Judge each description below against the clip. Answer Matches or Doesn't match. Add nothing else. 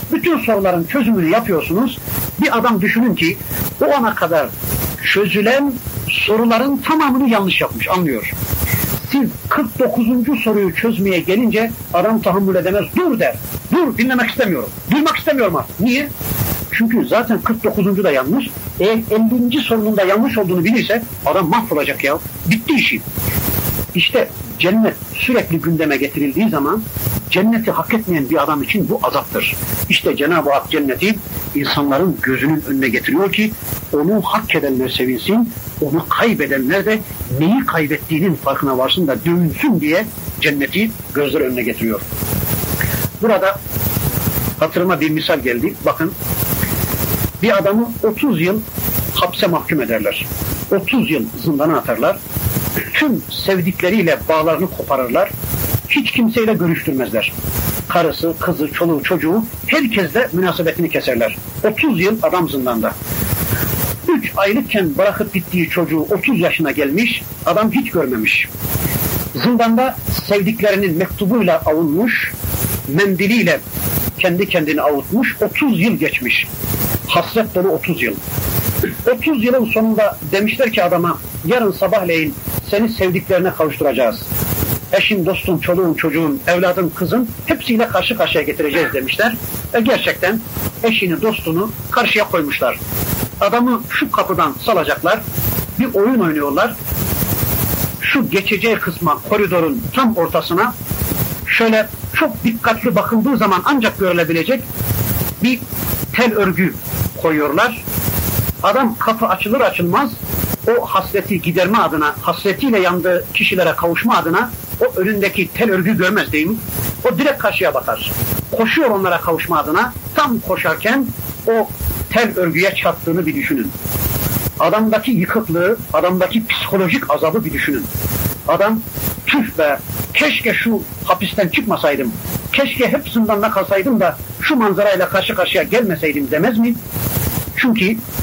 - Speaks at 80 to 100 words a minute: Doesn't match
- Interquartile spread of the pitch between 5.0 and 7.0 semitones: Matches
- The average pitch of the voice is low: Doesn't match